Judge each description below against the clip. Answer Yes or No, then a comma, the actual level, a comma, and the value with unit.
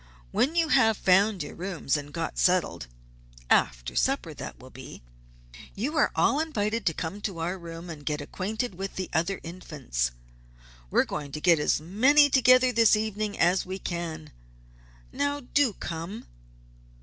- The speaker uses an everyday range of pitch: No, wide, 5.7 semitones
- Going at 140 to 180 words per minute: Yes, average, 160 wpm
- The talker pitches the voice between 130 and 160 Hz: No, high, 190 Hz